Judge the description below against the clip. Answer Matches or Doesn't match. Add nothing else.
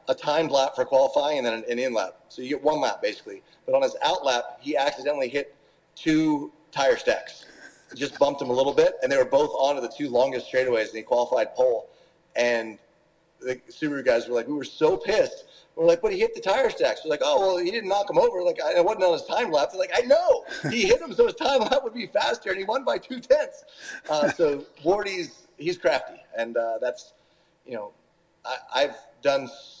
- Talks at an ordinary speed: Doesn't match